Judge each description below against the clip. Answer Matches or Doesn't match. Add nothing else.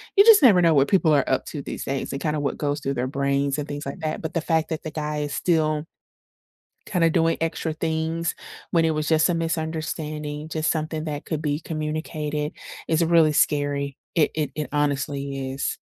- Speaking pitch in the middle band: Matches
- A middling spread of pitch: Doesn't match